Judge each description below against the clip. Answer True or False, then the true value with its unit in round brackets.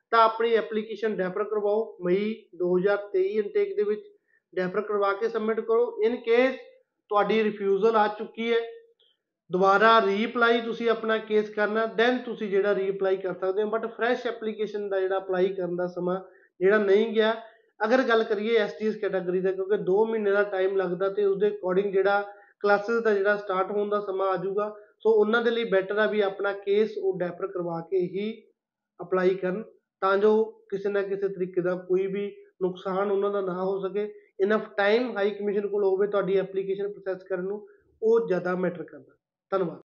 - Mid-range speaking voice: False (205 Hz)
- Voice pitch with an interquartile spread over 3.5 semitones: False (2.5 semitones)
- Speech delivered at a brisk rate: True (180 wpm)